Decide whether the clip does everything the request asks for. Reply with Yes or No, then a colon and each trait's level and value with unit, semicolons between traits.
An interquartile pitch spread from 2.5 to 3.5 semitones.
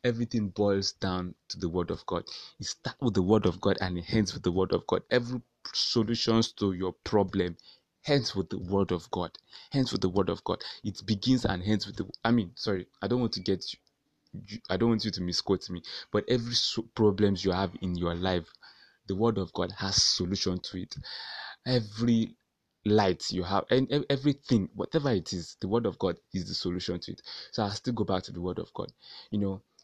No: average, 4.0 semitones